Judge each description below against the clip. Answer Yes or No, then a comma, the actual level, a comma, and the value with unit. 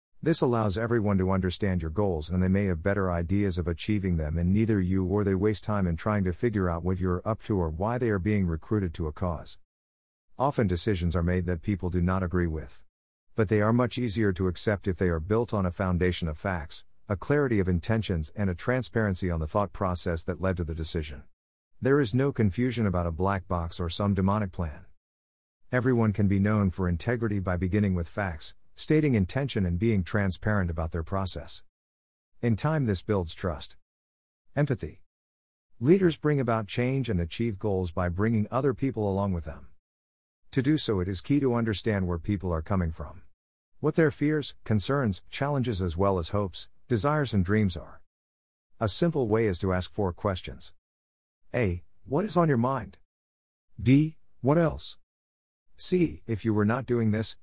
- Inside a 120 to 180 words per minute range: No, average, 190 wpm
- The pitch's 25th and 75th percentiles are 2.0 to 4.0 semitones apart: No, average, 4.5 semitones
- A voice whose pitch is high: No, very low, 95 Hz